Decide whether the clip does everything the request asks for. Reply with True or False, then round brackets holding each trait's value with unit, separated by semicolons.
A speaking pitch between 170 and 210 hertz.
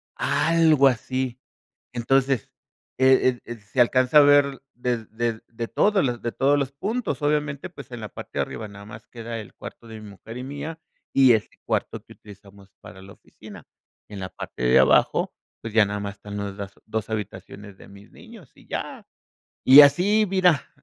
False (120 Hz)